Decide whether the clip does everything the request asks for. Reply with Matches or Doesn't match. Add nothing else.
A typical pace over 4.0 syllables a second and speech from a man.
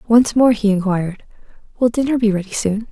Doesn't match